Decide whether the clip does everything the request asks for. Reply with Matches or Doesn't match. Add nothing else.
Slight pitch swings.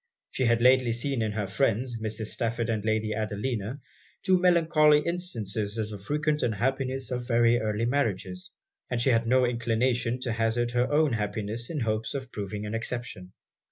Doesn't match